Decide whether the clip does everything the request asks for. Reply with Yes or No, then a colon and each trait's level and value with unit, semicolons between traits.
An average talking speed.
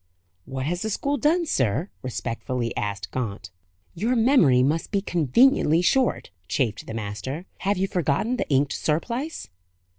Yes: average, 145 wpm